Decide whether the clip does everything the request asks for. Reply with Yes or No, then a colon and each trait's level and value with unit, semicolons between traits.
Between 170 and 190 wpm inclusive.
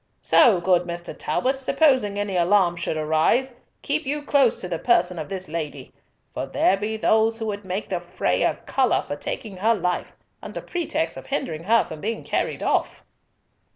Yes: average, 185 wpm